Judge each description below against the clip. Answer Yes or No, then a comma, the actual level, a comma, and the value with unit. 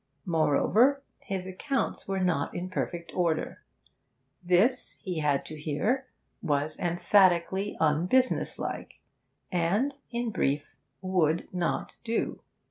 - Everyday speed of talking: No, slow, 105 wpm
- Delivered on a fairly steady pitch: No, average, 4.7 semitones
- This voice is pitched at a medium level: Yes, medium, 180 Hz